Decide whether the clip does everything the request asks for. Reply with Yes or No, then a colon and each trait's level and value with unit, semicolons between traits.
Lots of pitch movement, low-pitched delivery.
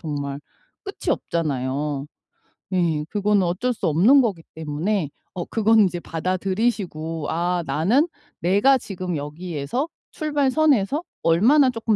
No: wide, 6.2 semitones; medium, 185 Hz